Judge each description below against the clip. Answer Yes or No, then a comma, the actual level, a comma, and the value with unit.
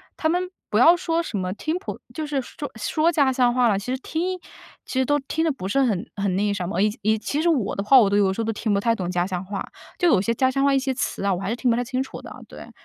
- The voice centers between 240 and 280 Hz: Yes, high, 245 Hz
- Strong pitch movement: Yes, wide, 6.2 semitones